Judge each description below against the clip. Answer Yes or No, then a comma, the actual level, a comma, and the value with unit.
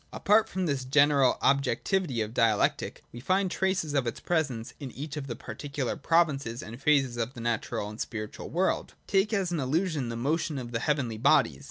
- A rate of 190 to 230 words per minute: Yes, average, 195 wpm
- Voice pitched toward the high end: No, medium, 140 Hz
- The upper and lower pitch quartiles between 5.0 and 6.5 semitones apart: Yes, wide, 5.6 semitones